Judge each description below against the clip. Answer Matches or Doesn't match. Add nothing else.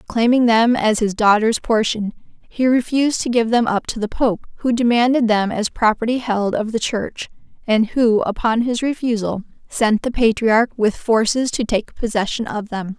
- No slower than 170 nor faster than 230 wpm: Matches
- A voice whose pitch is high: Matches